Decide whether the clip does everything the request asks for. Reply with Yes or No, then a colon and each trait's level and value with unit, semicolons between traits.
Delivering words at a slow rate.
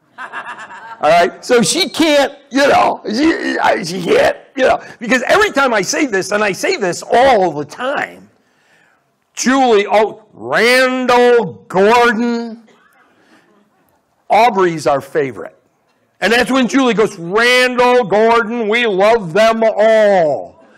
Yes: slow, 125 wpm